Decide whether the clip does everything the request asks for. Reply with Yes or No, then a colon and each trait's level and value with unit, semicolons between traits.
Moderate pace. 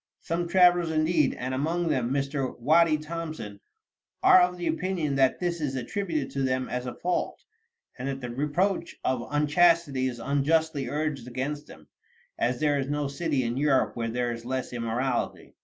Yes: average, 170 wpm